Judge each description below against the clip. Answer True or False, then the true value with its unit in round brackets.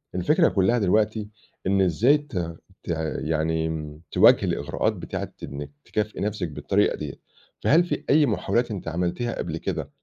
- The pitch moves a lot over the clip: True (6.5 semitones)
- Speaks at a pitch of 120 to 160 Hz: False (100 Hz)